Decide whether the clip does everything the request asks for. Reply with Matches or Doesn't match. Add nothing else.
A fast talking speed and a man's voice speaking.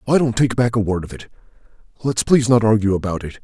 Matches